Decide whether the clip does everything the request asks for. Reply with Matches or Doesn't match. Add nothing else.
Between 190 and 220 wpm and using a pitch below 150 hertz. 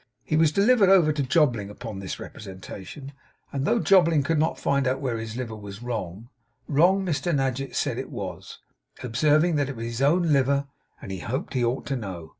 Matches